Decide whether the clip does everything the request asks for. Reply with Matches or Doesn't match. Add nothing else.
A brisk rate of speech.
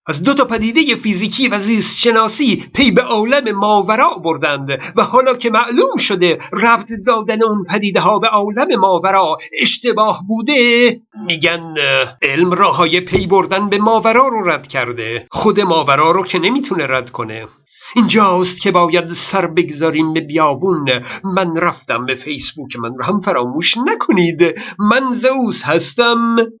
Doesn't match